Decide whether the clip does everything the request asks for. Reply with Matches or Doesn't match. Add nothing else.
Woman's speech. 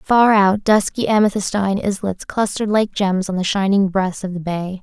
Matches